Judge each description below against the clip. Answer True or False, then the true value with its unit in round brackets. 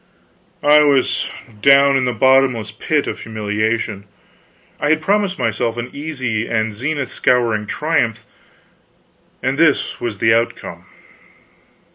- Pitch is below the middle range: True (120 Hz)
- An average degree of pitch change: True (4.5 semitones)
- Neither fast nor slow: False (120 wpm)